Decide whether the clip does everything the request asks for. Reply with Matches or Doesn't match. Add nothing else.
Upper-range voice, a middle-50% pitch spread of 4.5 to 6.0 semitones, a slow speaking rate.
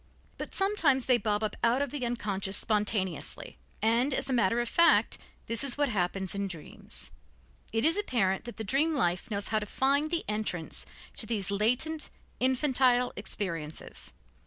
Doesn't match